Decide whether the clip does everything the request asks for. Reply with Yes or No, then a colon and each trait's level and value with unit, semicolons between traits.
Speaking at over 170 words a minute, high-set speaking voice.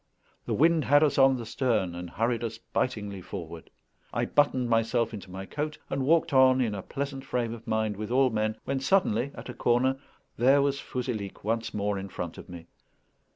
No: average, 200 wpm; low, 120 Hz